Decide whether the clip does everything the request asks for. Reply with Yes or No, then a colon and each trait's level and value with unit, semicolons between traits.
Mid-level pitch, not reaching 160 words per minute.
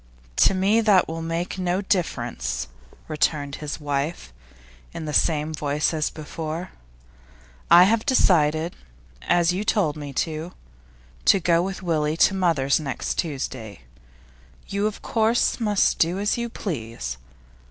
Yes: medium, 165 Hz; slow, 135 wpm